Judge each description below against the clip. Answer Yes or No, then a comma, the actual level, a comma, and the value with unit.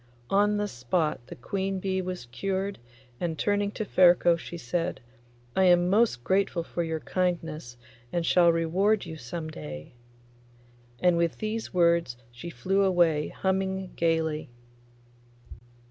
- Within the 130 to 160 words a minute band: Yes, slow, 135 wpm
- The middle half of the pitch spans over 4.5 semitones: No, average, 2.9 semitones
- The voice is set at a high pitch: No, medium, 175 Hz